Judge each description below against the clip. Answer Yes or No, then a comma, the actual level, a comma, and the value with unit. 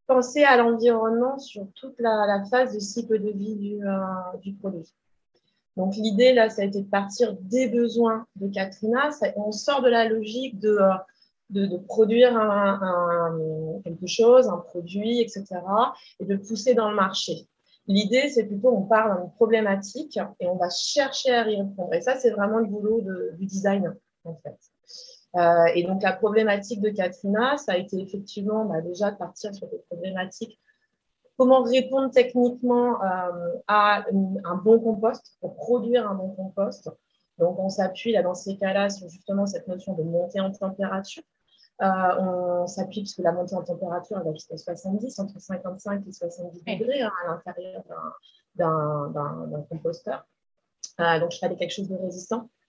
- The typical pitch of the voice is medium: No, high, 200 Hz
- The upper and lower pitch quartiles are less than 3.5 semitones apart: No, average, 4.1 semitones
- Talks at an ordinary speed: Yes, average, 180 wpm